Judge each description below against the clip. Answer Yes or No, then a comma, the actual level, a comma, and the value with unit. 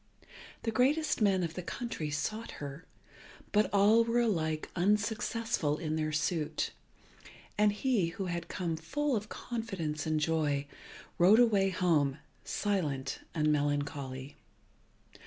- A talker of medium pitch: Yes, medium, 175 Hz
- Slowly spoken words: Yes, slow, 125 wpm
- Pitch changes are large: Yes, wide, 5.9 semitones